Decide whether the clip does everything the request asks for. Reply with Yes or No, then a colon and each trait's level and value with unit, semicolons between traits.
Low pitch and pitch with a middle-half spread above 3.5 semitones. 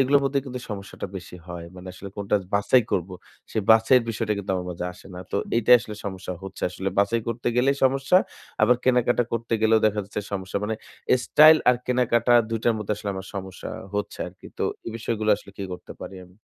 Yes: low, 110 Hz; average, 4.1 semitones